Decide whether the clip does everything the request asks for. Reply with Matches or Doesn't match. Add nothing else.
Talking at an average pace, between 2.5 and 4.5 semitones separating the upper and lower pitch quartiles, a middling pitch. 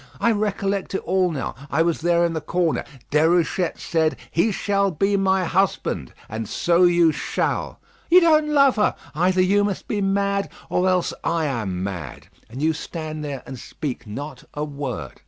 Doesn't match